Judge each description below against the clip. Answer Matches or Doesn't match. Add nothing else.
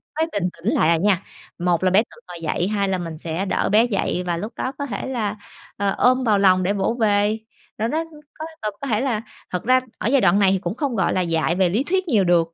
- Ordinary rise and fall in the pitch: Matches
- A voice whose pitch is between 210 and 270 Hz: Doesn't match